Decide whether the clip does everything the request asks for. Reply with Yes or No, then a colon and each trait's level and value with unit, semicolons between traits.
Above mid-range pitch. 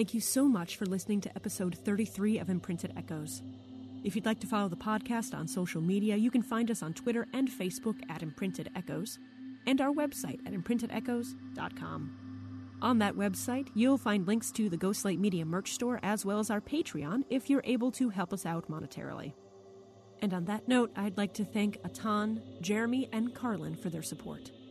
Yes: high, 210 Hz